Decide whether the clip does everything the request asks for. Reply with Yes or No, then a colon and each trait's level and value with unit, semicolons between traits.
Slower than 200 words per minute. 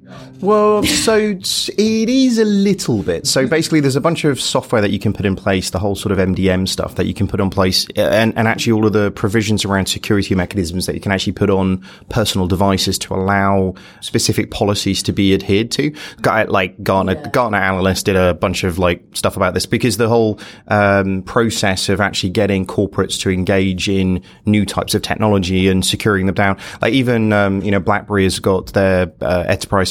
No: fast, 205 wpm